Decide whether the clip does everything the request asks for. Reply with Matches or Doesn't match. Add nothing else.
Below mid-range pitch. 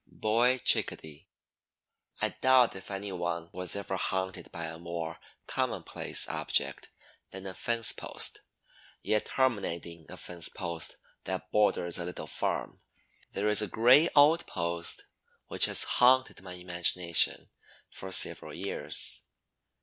Matches